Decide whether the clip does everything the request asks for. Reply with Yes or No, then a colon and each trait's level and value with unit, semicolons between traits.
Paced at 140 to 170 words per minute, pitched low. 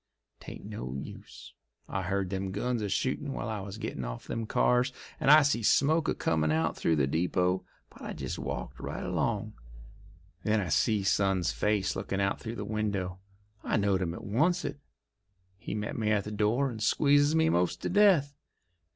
No: average, 185 wpm; low, 105 Hz